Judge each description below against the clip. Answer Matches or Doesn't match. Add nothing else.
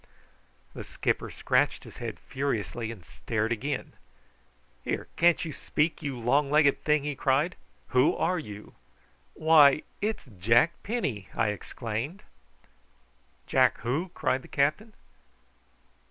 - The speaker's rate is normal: Doesn't match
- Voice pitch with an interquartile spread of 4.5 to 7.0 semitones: Matches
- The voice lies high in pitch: Doesn't match